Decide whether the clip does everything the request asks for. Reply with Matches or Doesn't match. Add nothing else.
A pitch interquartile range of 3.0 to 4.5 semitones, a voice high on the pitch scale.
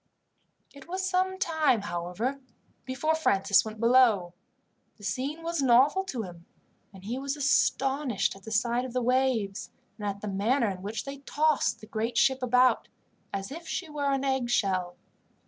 Doesn't match